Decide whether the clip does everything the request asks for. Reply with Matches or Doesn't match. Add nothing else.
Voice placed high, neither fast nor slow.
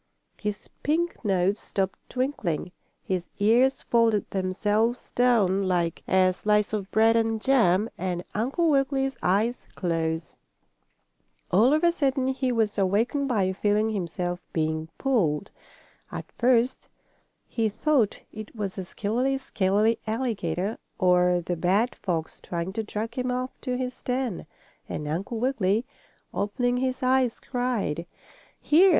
Doesn't match